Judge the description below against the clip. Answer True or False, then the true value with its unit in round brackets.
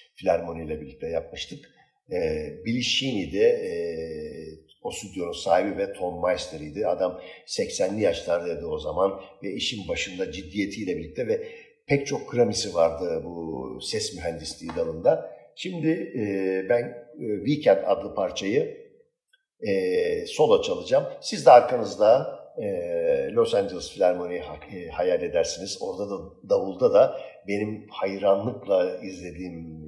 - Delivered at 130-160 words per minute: False (120 wpm)